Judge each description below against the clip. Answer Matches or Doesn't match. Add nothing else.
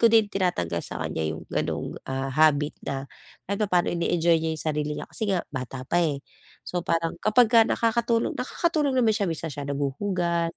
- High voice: Doesn't match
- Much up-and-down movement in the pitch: Matches